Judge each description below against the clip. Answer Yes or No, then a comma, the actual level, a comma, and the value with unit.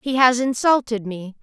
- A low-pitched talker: No, high, 240 Hz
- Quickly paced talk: No, average, 170 wpm